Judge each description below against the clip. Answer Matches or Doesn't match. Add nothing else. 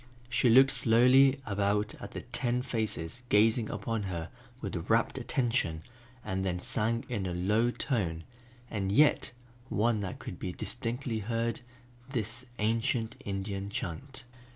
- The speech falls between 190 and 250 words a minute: Doesn't match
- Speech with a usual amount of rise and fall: Matches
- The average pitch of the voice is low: Matches